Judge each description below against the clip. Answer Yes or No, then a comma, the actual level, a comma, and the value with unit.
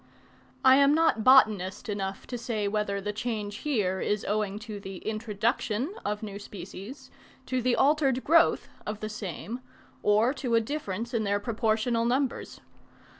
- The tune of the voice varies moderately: Yes, average, 3.4 semitones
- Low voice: No, high, 220 Hz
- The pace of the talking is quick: No, average, 155 wpm